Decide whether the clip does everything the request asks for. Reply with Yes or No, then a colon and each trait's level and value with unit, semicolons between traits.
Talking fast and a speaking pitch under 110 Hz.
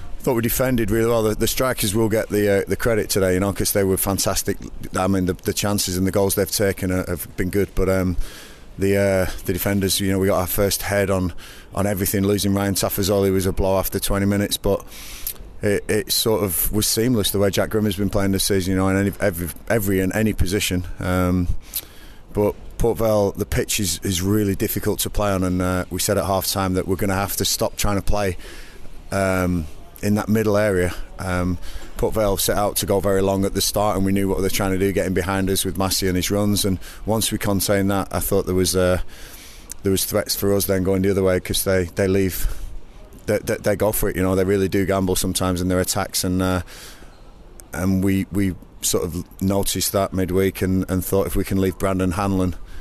Yes: fast, 235 wpm; very low, 95 Hz